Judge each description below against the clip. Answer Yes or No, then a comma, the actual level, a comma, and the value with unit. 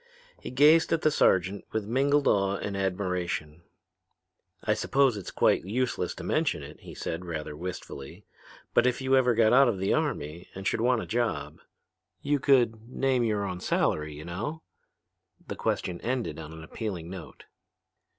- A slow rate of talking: No, average, 170 wpm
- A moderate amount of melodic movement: No, wide, 6.0 semitones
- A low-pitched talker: Yes, low, 105 Hz